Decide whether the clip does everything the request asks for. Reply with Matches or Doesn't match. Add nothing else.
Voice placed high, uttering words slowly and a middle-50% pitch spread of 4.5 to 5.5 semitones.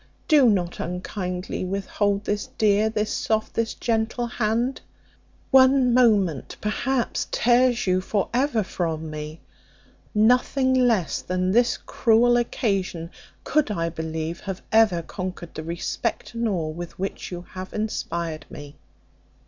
Matches